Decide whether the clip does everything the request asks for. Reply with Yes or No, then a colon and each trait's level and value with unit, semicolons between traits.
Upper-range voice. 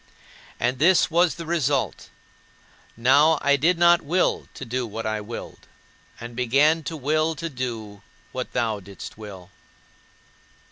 No: low, 135 Hz